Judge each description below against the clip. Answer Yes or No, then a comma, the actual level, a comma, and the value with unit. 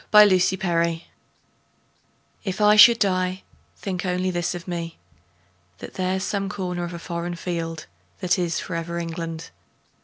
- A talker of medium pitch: Yes, medium, 180 Hz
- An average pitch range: No, narrow, 1.9 semitones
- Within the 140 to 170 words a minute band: Yes, average, 145 wpm